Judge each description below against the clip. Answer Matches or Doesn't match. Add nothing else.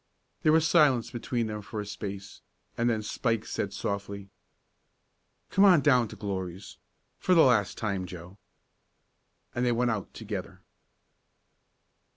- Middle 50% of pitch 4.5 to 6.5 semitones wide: Doesn't match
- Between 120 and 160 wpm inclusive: Matches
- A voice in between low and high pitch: Doesn't match